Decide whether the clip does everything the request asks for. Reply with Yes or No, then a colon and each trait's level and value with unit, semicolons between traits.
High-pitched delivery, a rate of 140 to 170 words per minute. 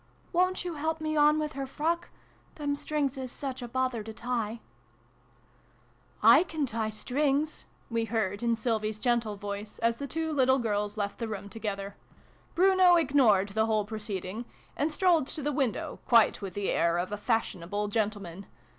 No: high, 235 Hz; average, 180 wpm